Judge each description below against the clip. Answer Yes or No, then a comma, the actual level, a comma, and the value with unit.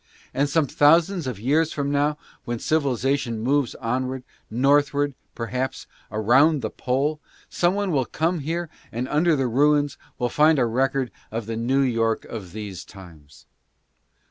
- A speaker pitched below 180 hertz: Yes, low, 135 Hz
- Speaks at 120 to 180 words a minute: Yes, average, 160 wpm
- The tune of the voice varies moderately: Yes, average, 4.2 semitones